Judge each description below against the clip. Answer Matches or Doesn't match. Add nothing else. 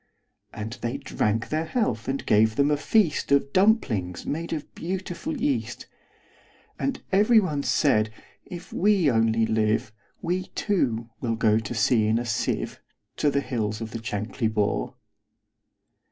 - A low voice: Matches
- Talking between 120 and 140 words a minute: Matches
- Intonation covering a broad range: Matches